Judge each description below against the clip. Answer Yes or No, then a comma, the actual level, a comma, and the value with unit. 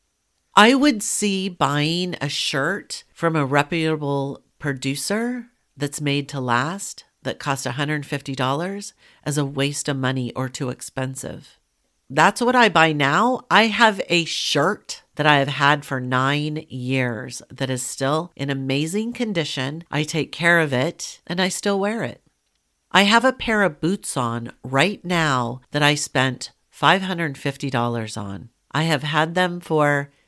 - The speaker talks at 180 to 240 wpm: No, average, 150 wpm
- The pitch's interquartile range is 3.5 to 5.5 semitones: Yes, average, 4.8 semitones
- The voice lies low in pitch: No, medium, 150 Hz